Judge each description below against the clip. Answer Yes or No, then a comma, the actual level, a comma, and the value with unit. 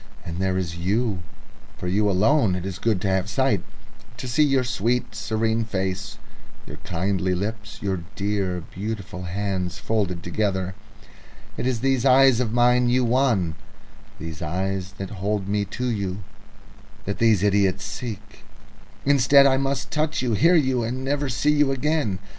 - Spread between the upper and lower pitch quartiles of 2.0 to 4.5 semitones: No, average, 4.9 semitones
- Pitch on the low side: Yes, low, 105 Hz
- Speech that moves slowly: No, average, 160 wpm